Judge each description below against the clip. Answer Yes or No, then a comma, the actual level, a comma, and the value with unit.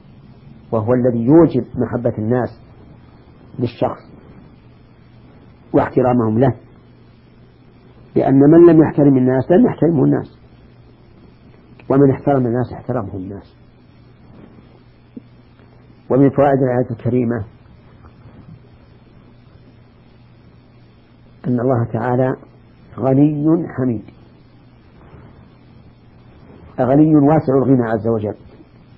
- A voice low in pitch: Yes, low, 125 Hz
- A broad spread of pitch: No, narrow, 2.6 semitones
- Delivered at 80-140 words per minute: No, average, 70 wpm